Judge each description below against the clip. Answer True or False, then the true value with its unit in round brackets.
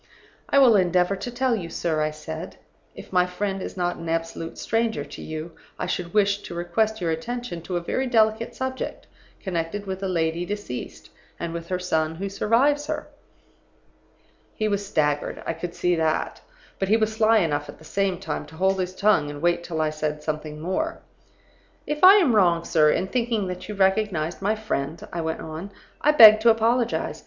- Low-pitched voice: False (185 Hz)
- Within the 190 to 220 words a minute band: True (195 wpm)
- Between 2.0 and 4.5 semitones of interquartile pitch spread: False (4.9 semitones)